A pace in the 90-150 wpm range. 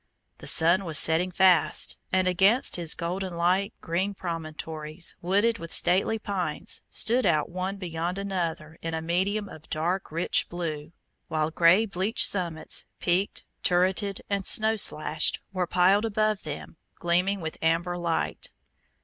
Yes: average, 140 wpm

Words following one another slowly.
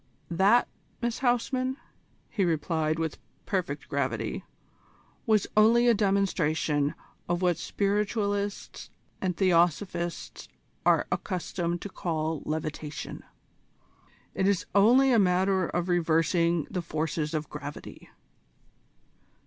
Yes: slow, 100 wpm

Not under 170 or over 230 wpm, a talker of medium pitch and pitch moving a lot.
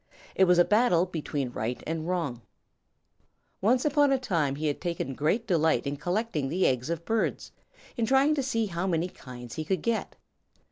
Yes: average, 185 wpm; medium, 175 Hz; wide, 7.0 semitones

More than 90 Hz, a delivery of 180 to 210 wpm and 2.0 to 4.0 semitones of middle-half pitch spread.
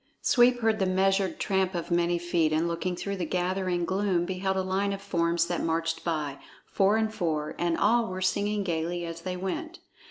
Yes: medium, 185 Hz; average, 195 wpm; narrow, 2.6 semitones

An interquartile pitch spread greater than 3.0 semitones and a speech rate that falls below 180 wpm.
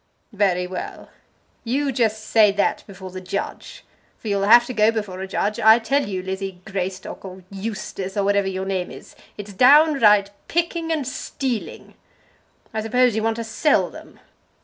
Yes: average, 3.5 semitones; average, 170 wpm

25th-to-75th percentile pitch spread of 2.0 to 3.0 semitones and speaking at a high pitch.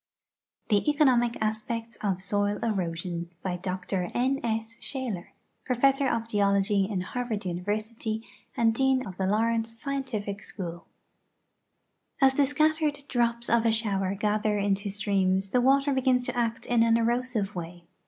No: average, 3.8 semitones; high, 225 Hz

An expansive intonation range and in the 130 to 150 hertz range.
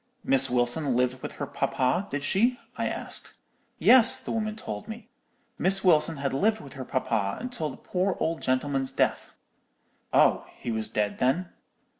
Yes: wide, 7.0 semitones; medium, 140 Hz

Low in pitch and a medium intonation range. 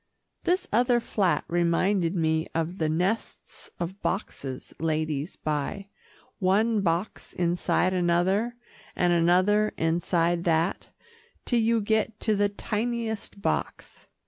No: medium, 185 Hz; average, 4.2 semitones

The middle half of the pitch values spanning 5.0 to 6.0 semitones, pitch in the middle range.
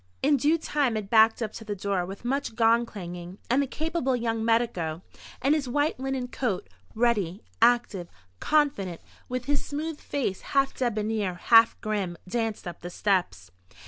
No: wide, 5.4 semitones; high, 230 Hz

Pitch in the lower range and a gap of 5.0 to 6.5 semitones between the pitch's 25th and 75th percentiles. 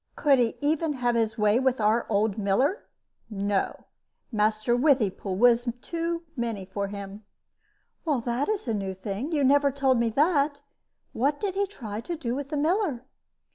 No: high, 245 Hz; average, 5.3 semitones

